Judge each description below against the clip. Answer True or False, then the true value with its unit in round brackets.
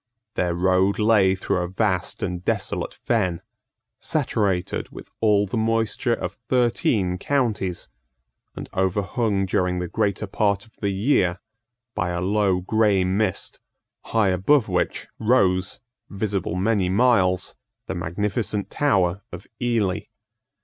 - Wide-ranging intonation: False (3.1 semitones)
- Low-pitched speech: True (100 Hz)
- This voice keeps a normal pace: False (125 wpm)